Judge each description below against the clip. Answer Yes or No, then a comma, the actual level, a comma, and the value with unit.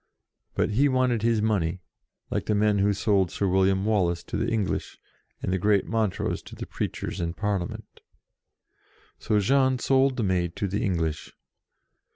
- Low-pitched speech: Yes, low, 105 Hz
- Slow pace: No, average, 165 wpm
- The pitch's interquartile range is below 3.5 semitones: Yes, average, 3.1 semitones